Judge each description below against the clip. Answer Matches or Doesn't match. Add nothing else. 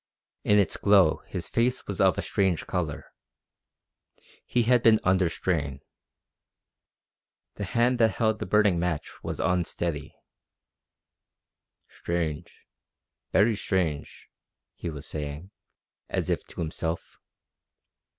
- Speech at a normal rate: Doesn't match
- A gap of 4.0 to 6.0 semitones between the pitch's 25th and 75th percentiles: Matches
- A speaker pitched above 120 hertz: Doesn't match